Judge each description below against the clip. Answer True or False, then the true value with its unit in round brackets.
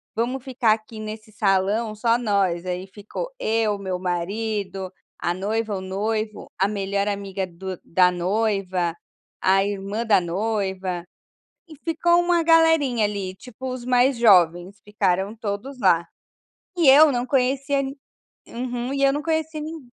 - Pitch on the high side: True (215 Hz)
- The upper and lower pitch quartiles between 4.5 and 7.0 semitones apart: True (4.8 semitones)